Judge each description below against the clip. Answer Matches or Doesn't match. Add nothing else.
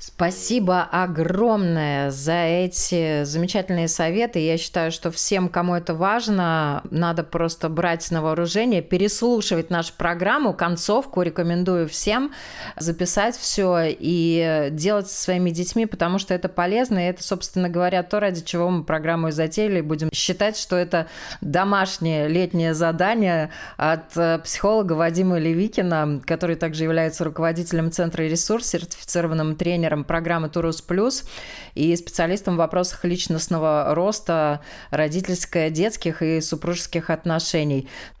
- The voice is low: Doesn't match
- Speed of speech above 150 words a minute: Doesn't match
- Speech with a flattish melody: Matches